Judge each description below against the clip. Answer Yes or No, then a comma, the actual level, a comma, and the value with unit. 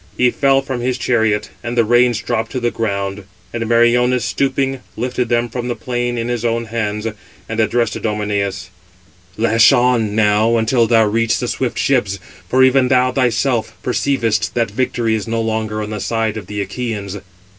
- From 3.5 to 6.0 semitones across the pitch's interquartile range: No, narrow, 2.4 semitones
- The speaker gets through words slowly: No, average, 175 wpm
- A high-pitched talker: No, low, 115 Hz